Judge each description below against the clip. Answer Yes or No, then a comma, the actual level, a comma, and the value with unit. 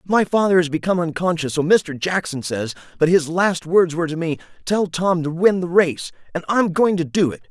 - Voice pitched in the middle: Yes, medium, 170 Hz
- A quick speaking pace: Yes, fast, 225 wpm